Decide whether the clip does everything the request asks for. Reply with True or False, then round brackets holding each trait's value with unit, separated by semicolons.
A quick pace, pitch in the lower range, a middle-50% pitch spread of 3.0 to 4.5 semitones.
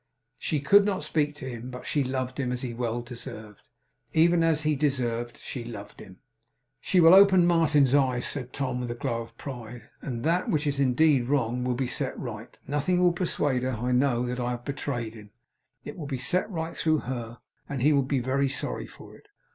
True (210 wpm; 130 Hz; 3.8 semitones)